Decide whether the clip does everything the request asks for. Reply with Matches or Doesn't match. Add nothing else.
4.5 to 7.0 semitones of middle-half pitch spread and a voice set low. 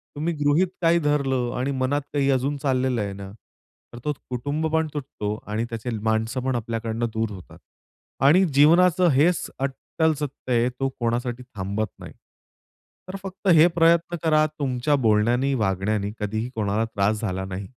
Matches